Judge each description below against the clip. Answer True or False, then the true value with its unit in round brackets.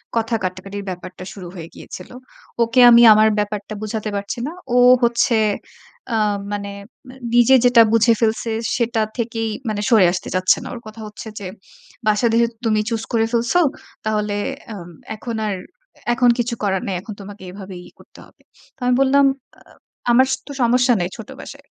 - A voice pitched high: True (220 Hz)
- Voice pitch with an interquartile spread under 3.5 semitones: True (2.8 semitones)